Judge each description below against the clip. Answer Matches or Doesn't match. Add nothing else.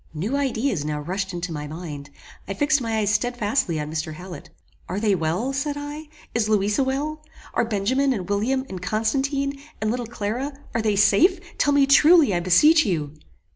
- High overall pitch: Matches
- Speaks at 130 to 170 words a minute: Doesn't match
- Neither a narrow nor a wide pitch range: Doesn't match